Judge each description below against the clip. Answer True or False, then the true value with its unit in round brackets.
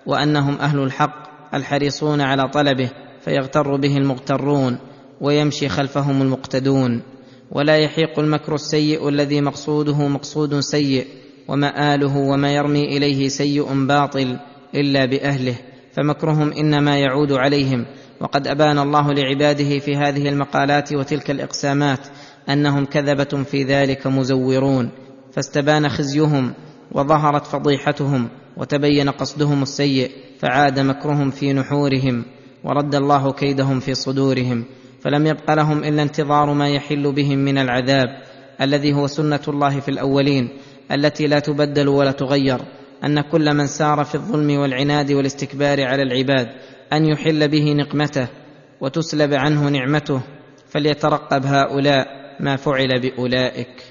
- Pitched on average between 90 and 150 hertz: True (140 Hz)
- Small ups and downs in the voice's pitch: True (1.4 semitones)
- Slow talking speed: False (115 wpm)